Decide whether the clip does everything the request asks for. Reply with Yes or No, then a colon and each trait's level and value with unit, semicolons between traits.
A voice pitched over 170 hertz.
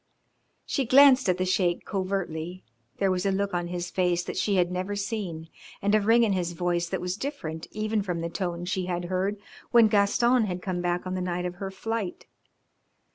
Yes: medium, 185 Hz